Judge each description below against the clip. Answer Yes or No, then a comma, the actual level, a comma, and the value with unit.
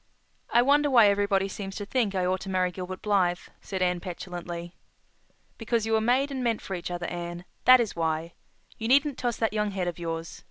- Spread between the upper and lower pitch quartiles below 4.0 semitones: No, average, 4.4 semitones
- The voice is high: Yes, high, 195 Hz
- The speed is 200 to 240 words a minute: Yes, fast, 205 wpm